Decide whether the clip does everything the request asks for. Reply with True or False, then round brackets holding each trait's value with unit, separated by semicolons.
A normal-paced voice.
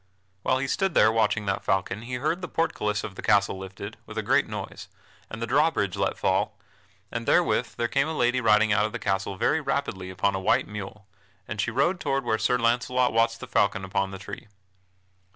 False (210 wpm)